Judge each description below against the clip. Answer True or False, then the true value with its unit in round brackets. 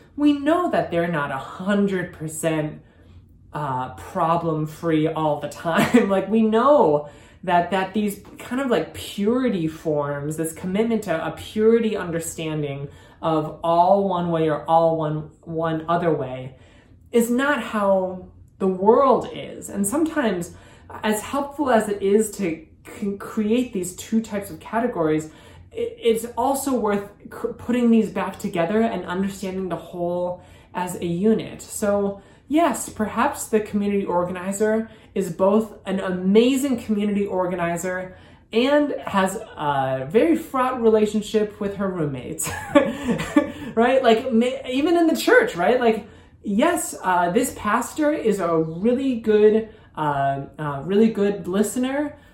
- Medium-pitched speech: False (200 Hz)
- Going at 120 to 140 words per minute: True (135 wpm)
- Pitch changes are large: True (5.7 semitones)